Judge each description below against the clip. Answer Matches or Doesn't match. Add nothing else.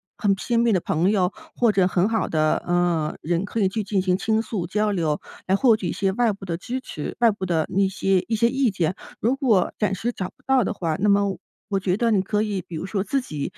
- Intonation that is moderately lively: Matches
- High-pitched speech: Matches